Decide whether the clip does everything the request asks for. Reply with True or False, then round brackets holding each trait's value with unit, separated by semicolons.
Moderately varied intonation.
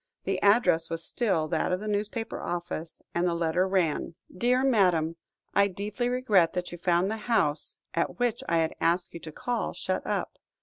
True (4.3 semitones)